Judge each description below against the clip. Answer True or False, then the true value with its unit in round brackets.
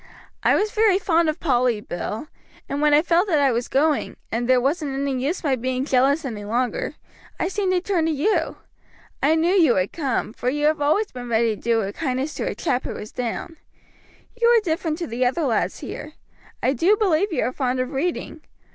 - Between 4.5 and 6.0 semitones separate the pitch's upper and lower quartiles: True (5.2 semitones)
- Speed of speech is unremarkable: False (220 wpm)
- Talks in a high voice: True (290 Hz)